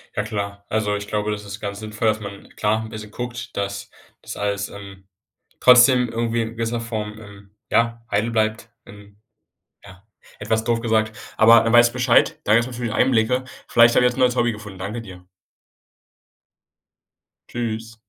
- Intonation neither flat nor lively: No, narrow, 2.3 semitones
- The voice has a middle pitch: No, low, 110 Hz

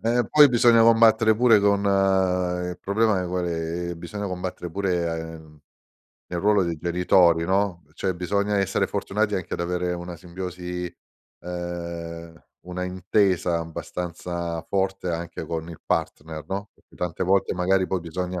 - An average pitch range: No, narrow, 2.3 semitones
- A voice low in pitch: Yes, very low, 90 Hz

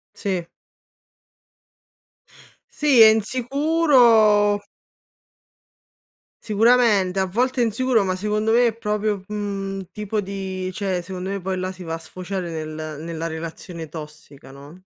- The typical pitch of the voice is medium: No, high, 195 Hz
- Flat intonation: No, average, 3.6 semitones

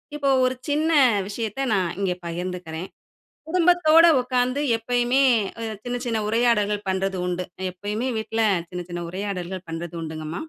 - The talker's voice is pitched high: Yes, high, 205 Hz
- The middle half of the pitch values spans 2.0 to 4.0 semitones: No, wide, 5.6 semitones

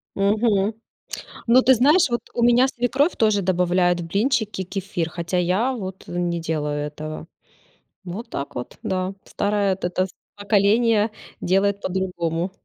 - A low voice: No, high, 195 Hz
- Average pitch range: Yes, average, 4.1 semitones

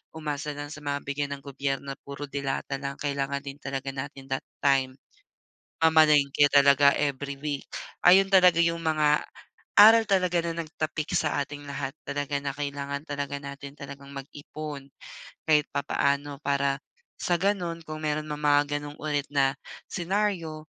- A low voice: No, medium, 145 Hz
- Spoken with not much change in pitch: Yes, narrow, 1.7 semitones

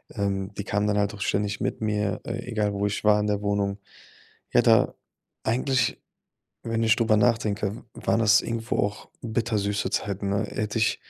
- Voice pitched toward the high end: No, low, 105 Hz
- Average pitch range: No, narrow, 1.7 semitones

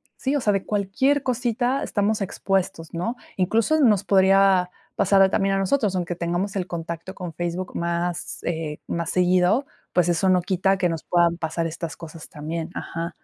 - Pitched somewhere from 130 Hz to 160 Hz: No, medium, 185 Hz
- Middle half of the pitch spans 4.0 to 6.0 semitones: No, average, 2.8 semitones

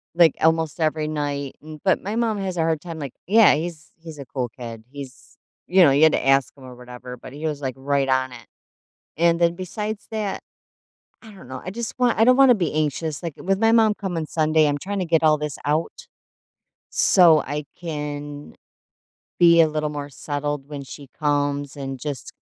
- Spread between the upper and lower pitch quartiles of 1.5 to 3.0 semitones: No, average, 3.7 semitones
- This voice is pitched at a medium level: Yes, medium, 155 Hz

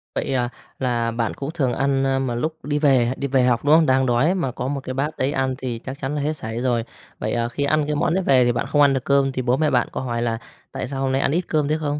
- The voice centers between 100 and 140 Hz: Yes, low, 135 Hz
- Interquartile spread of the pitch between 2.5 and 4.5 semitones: Yes, average, 2.9 semitones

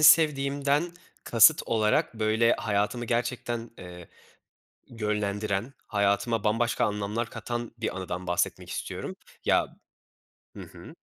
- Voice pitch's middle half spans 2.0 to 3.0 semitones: Yes, average, 2.7 semitones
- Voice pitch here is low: Yes, low, 115 Hz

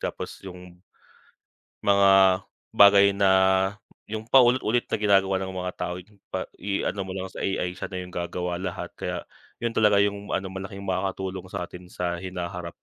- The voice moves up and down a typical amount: No, narrow, 1.9 semitones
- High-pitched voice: No, very low, 95 Hz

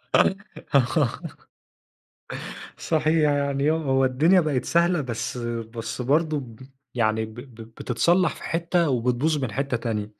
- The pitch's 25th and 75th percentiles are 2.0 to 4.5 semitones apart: No, average, 5.1 semitones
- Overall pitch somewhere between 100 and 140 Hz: Yes, low, 135 Hz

